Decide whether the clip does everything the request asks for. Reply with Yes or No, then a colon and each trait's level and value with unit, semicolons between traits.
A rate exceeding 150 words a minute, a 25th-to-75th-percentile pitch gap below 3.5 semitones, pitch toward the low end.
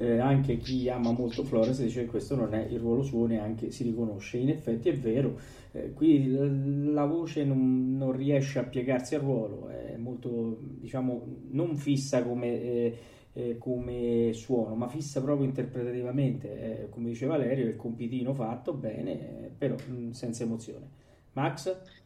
Yes: average, 160 wpm; narrow, 2.6 semitones; low, 125 Hz